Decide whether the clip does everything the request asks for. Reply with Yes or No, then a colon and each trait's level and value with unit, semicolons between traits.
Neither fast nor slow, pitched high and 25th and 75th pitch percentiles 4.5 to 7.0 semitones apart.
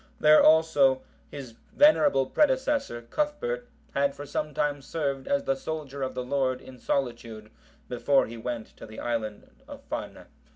No: average, 155 wpm; medium, 140 Hz; average, 4.9 semitones